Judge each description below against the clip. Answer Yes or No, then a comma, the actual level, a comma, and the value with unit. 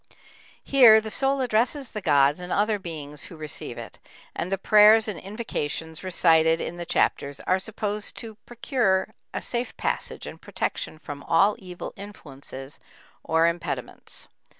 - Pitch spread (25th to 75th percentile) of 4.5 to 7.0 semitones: Yes, average, 5.2 semitones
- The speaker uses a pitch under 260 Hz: Yes, medium, 185 Hz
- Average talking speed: Yes, average, 150 wpm